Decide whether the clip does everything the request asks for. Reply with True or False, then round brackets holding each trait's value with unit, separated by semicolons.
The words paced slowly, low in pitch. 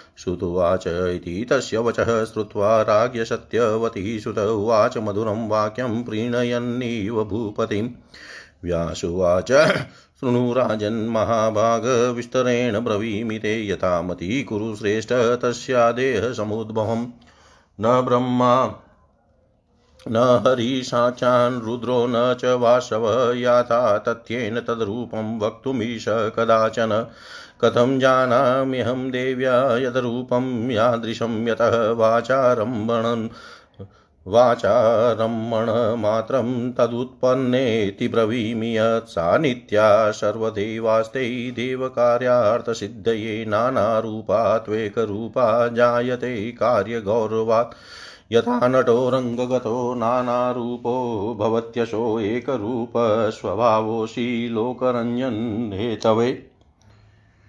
True (55 wpm; 115 Hz)